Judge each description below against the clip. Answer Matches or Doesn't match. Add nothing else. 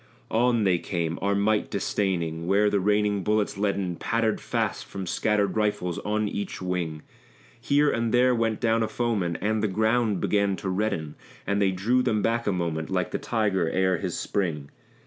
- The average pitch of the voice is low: Matches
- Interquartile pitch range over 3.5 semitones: Doesn't match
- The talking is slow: Doesn't match